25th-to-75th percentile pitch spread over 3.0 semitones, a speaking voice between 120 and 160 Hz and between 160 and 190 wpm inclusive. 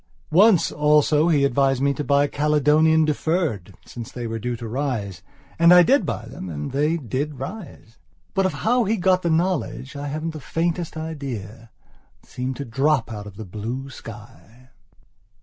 Yes: average, 5.1 semitones; medium, 140 Hz; average, 175 wpm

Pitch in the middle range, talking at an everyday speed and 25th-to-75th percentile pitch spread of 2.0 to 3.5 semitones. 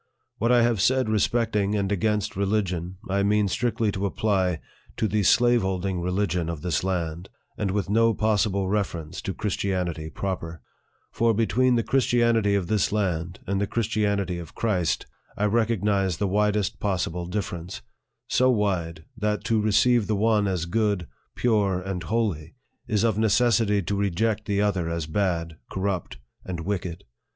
No: low, 100 Hz; average, 160 wpm; average, 3.1 semitones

